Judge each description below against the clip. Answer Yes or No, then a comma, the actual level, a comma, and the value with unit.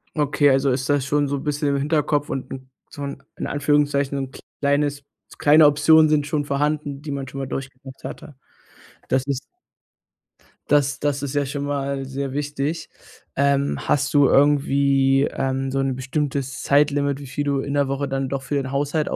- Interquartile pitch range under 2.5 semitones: Yes, narrow, 1.3 semitones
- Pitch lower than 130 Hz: No, medium, 140 Hz